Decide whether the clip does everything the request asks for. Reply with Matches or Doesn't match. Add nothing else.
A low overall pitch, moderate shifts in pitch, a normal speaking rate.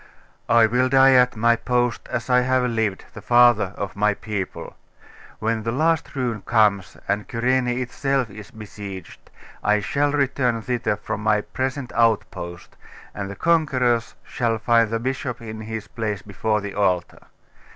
Matches